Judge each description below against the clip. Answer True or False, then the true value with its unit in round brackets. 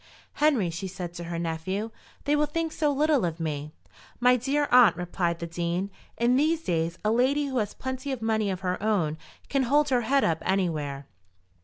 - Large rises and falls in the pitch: True (7.9 semitones)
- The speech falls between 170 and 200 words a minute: True (195 wpm)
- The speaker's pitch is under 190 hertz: False (210 Hz)